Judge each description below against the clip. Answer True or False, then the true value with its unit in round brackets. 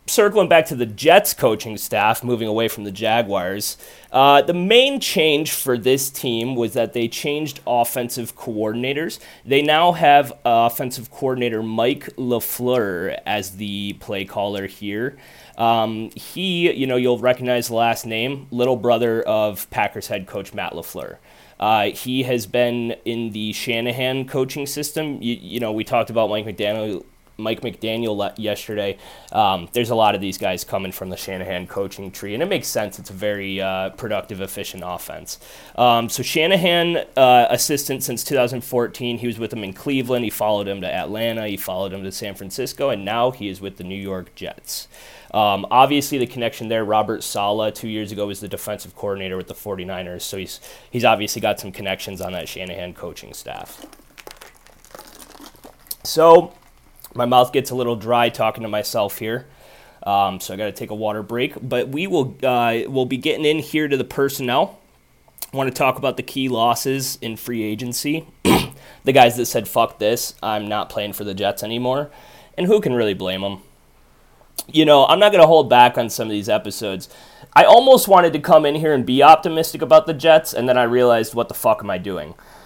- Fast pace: False (185 wpm)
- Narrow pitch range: False (4.0 semitones)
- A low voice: True (120 Hz)